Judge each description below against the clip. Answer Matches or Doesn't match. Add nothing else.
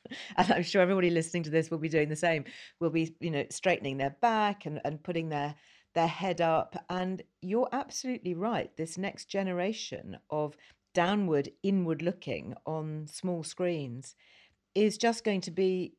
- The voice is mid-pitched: Matches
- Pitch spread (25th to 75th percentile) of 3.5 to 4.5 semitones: Matches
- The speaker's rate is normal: Matches